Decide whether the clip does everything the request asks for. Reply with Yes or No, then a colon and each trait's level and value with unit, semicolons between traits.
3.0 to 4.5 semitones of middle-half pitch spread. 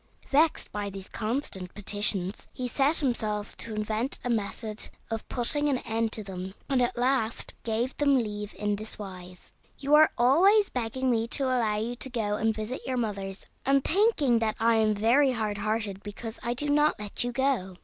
Yes: average, 3.9 semitones